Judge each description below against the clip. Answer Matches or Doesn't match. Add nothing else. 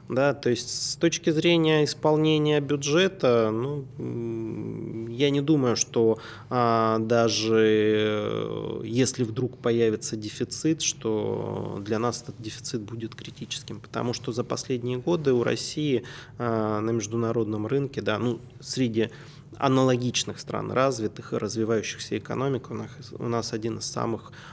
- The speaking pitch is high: Doesn't match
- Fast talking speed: Doesn't match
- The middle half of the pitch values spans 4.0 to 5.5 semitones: Doesn't match